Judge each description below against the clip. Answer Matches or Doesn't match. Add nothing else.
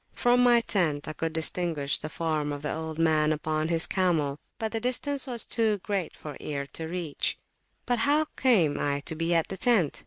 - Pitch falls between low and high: Matches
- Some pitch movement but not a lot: Doesn't match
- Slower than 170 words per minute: Doesn't match